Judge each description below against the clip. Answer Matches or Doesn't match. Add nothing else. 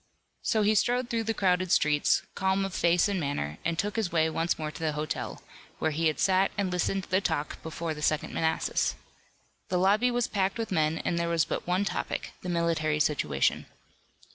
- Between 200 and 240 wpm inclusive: Matches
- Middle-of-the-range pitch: Matches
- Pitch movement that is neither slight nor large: Matches